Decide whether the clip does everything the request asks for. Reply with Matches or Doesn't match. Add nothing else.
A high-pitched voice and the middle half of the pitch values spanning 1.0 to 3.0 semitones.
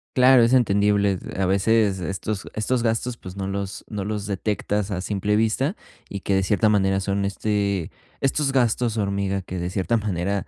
Doesn't match